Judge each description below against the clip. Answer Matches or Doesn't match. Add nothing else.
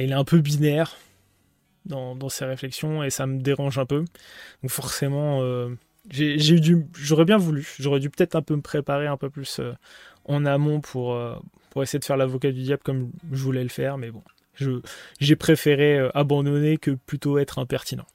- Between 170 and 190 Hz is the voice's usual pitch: Doesn't match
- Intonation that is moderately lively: Doesn't match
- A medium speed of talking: Matches